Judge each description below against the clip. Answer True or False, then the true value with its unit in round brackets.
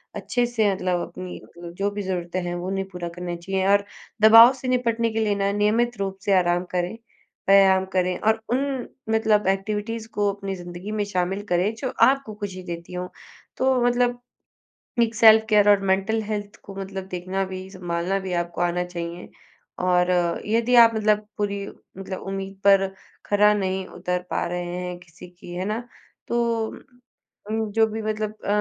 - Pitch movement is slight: False (3.1 semitones)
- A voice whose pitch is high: True (195 Hz)